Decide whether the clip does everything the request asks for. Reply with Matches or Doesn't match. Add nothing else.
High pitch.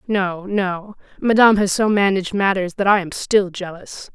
Matches